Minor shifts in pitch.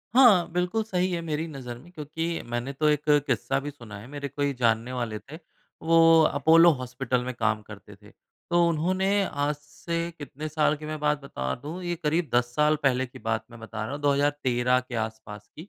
No: average, 4.7 semitones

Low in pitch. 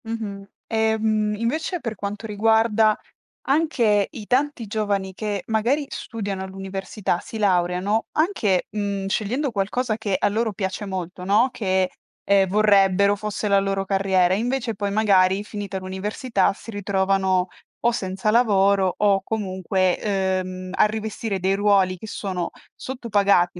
No: high, 205 Hz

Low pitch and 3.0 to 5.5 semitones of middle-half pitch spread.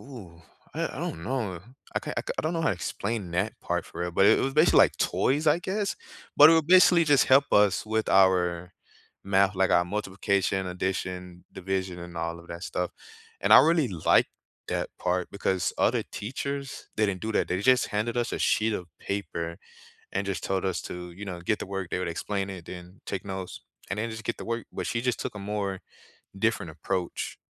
Yes: low, 100 Hz; average, 4.2 semitones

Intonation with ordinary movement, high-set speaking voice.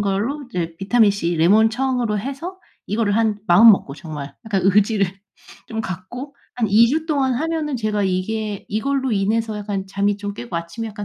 Yes: average, 3.7 semitones; high, 215 Hz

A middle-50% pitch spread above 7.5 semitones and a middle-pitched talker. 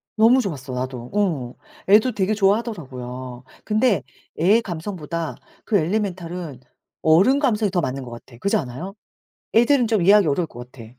Yes: wide, 8.3 semitones; medium, 175 Hz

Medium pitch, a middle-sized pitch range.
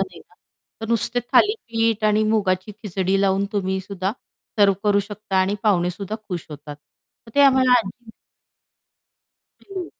No: high, 205 Hz; average, 3.0 semitones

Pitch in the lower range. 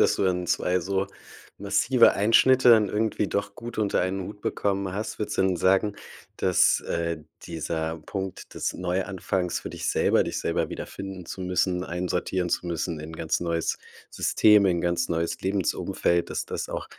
Yes: very low, 95 Hz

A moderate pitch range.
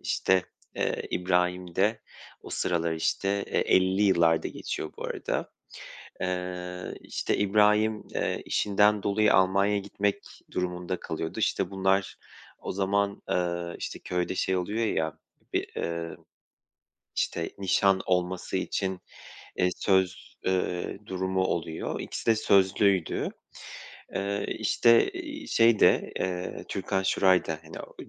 No: narrow, 2.0 semitones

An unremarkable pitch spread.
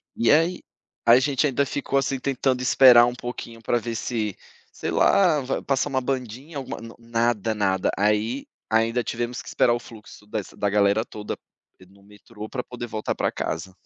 Yes: average, 3.5 semitones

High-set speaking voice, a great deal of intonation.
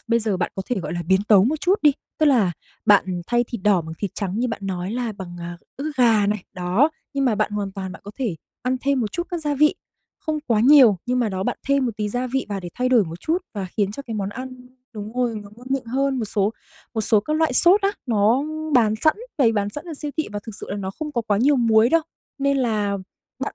No: high, 225 Hz; average, 4.9 semitones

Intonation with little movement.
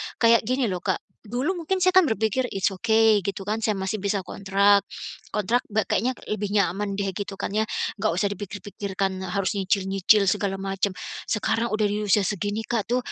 Yes: narrow, 2.3 semitones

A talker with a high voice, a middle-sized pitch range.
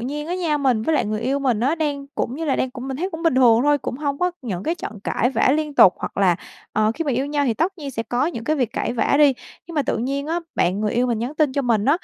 Yes: very high, 275 Hz; average, 4.2 semitones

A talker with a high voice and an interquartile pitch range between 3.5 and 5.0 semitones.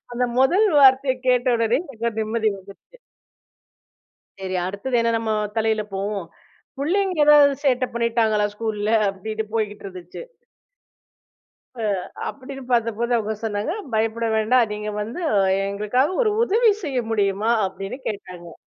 Yes: high, 225 Hz; average, 3.9 semitones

